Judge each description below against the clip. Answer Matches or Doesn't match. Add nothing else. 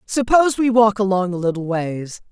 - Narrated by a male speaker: Doesn't match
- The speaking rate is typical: Matches